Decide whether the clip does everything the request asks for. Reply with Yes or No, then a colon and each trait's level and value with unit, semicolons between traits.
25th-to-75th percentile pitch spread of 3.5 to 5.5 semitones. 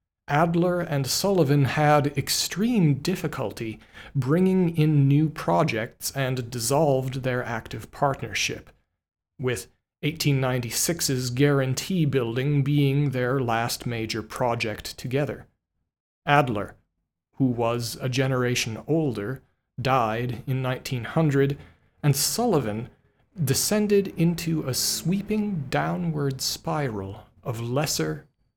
Yes: average, 4.1 semitones